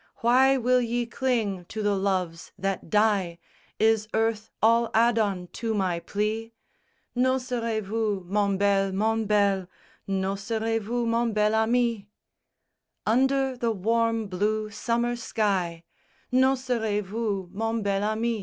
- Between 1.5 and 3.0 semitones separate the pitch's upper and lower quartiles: Yes, average, 2.7 semitones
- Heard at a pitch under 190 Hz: No, high, 220 Hz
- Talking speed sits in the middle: No, slow, 125 wpm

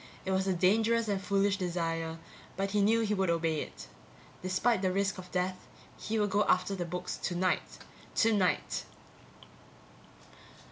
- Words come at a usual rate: Yes, average, 150 wpm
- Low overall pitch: No, high, 190 Hz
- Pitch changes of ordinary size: No, narrow, 2.1 semitones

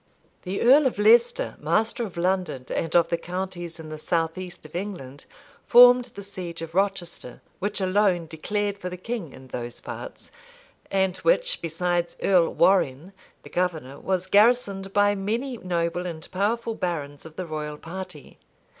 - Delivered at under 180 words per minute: Yes, average, 160 wpm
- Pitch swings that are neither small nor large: Yes, average, 3.6 semitones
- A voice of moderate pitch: Yes, medium, 180 Hz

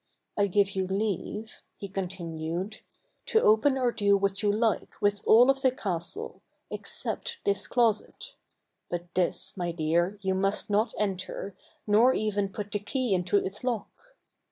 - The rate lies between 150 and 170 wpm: Yes, average, 160 wpm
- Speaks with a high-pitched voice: Yes, high, 205 Hz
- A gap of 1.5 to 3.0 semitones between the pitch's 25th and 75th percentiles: Yes, average, 2.7 semitones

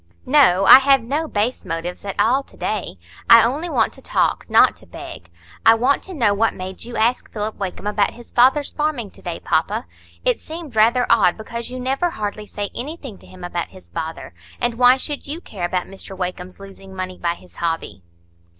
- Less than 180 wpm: No, fast, 205 wpm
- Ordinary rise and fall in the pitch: No, wide, 5.7 semitones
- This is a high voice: Yes, high, 220 Hz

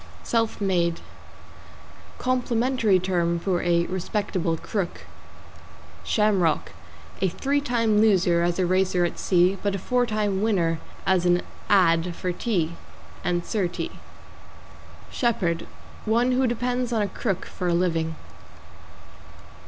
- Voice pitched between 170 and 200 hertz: Yes, high, 190 Hz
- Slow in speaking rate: Yes, slow, 125 wpm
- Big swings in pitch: No, average, 4.4 semitones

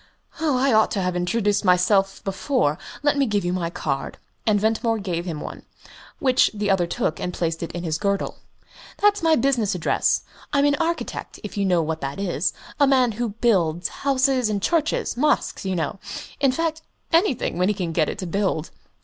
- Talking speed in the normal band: Yes, average, 190 wpm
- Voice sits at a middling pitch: No, high, 205 Hz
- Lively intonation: Yes, wide, 6.7 semitones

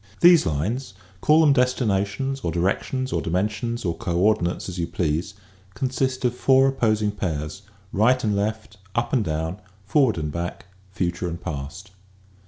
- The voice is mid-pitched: No, low, 100 Hz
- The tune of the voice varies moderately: No, wide, 6.2 semitones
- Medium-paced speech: Yes, average, 165 wpm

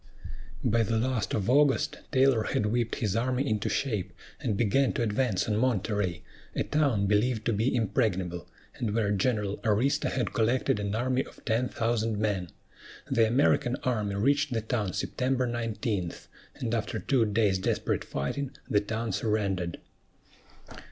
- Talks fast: No, average, 150 wpm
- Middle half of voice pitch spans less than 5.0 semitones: Yes, average, 3.5 semitones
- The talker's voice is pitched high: No, low, 110 Hz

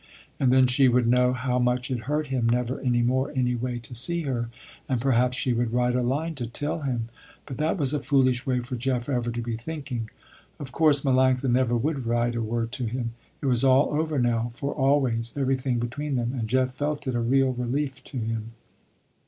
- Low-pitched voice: Yes, low, 125 Hz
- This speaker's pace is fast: Yes, fast, 215 wpm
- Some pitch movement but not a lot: No, narrow, 2.2 semitones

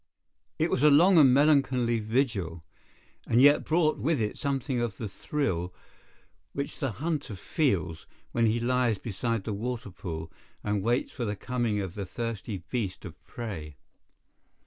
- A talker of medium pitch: No, low, 115 Hz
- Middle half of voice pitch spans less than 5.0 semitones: No, average, 5.3 semitones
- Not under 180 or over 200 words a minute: No, average, 155 wpm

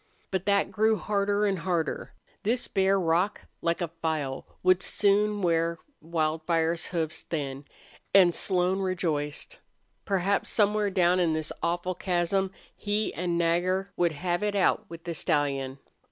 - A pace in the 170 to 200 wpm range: No, average, 140 wpm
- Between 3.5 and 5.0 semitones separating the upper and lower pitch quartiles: No, average, 3.1 semitones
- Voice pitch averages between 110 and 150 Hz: No, medium, 175 Hz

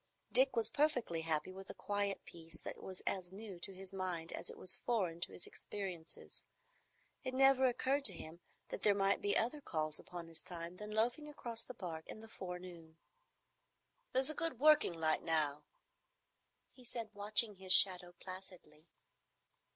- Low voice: No, high, 190 Hz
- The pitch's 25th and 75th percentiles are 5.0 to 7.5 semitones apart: Yes, average, 5.3 semitones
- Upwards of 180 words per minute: No, average, 170 wpm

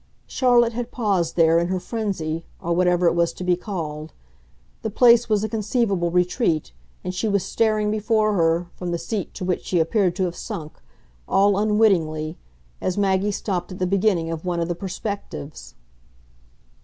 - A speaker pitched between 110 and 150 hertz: No, medium, 185 Hz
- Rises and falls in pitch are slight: No, average, 3.8 semitones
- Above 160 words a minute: Yes, average, 180 wpm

